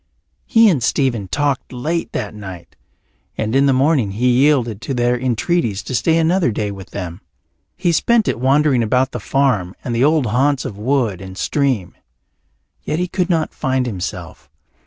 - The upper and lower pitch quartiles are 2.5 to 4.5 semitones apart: No, wide, 5.4 semitones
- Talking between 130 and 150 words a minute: No, average, 175 wpm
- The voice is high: No, low, 130 Hz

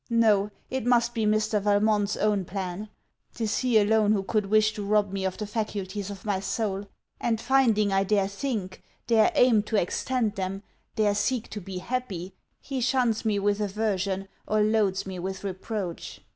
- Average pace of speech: Yes, average, 175 wpm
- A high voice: Yes, high, 210 Hz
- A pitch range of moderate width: No, narrow, 2.2 semitones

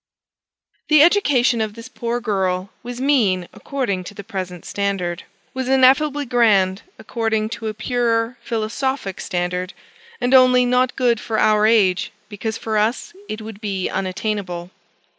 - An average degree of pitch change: Yes, average, 4.2 semitones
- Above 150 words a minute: No, average, 140 wpm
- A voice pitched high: Yes, high, 220 Hz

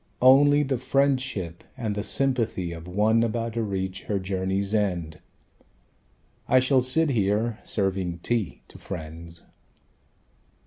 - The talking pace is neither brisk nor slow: No, slow, 125 wpm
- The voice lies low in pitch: Yes, low, 105 Hz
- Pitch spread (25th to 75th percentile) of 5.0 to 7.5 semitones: Yes, wide, 5.4 semitones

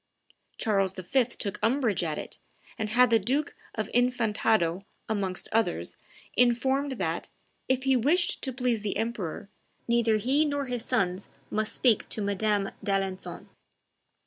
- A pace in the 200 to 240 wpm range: No, average, 140 wpm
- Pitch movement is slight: No, average, 4.1 semitones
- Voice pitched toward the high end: Yes, high, 225 Hz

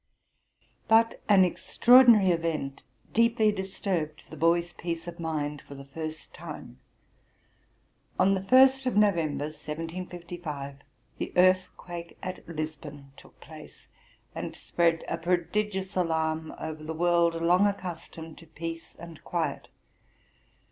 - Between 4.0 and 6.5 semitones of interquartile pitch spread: No, average, 3.1 semitones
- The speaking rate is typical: No, slow, 120 wpm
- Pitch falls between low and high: Yes, medium, 170 Hz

